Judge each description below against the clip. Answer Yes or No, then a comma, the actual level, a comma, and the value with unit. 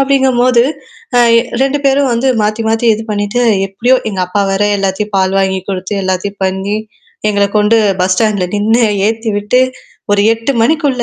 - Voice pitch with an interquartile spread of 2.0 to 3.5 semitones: No, average, 3.9 semitones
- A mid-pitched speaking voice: No, high, 215 Hz